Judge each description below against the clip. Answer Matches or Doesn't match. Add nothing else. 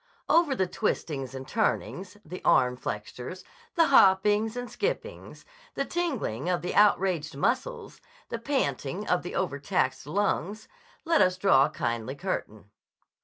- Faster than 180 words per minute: Doesn't match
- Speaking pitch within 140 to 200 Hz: Matches